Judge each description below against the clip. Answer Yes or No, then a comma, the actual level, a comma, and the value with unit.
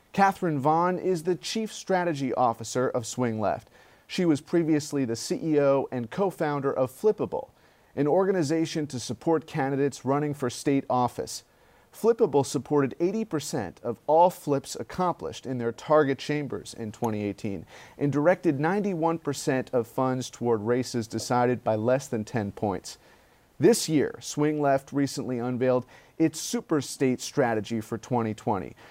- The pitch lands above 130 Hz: Yes, medium, 140 Hz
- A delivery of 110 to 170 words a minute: Yes, average, 140 wpm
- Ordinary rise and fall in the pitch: Yes, average, 4.7 semitones